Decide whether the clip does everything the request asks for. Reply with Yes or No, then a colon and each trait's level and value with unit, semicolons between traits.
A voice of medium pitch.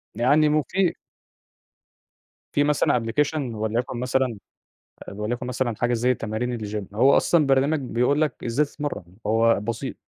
No: low, 125 Hz